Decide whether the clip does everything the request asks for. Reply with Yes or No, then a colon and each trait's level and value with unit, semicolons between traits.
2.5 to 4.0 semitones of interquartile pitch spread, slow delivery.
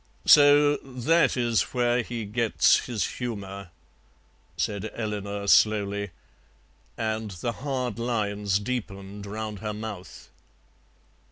Yes: average, 3.2 semitones; slow, 100 wpm